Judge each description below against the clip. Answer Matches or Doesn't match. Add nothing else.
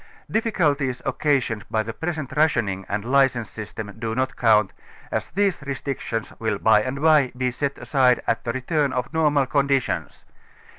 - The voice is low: Matches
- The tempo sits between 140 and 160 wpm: Matches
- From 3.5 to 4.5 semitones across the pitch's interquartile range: Matches